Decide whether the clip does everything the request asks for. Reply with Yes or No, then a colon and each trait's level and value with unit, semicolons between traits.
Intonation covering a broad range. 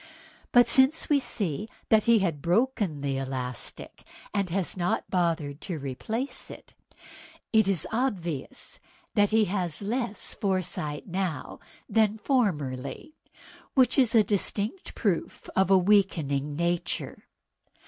Yes: wide, 5.8 semitones